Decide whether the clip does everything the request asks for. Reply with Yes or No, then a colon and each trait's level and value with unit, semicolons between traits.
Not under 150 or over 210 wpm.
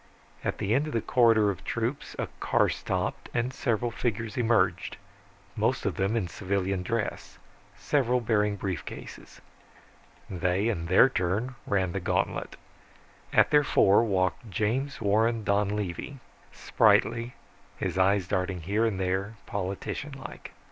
No: slow, 135 wpm